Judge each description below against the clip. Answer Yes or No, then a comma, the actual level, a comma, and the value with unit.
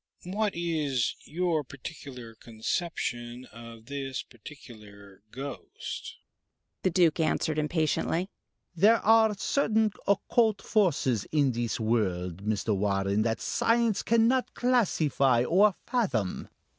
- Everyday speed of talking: No, slow, 105 wpm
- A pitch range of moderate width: No, wide, 8.8 semitones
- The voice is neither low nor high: Yes, medium, 145 Hz